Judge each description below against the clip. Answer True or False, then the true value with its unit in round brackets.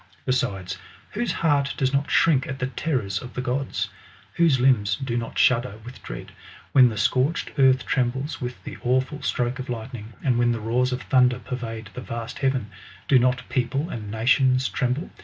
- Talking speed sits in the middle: True (180 wpm)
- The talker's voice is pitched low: True (125 Hz)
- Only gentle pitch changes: True (2.0 semitones)